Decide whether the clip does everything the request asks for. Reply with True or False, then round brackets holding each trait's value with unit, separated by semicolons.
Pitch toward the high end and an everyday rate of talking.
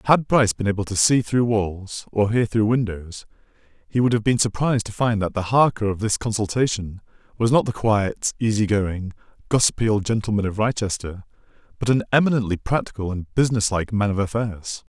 False (110 Hz; 185 wpm)